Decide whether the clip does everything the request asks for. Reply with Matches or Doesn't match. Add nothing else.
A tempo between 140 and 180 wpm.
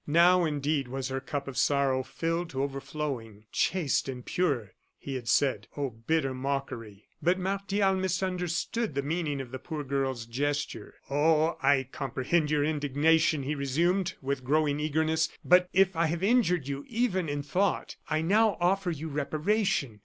Matches